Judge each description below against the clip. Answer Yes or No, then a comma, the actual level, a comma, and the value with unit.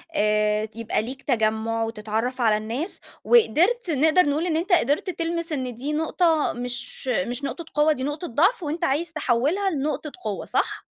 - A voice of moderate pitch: No, very high, 285 Hz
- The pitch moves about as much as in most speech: No, wide, 6.1 semitones